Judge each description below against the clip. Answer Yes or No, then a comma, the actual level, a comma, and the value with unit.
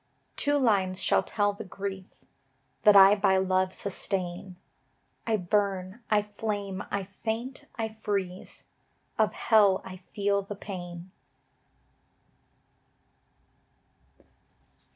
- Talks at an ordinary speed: No, slow, 100 wpm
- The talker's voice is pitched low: No, high, 200 Hz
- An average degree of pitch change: No, narrow, 1.9 semitones